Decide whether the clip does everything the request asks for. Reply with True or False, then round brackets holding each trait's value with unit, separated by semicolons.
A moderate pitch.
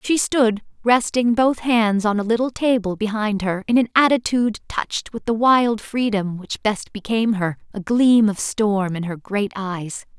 False (220 Hz)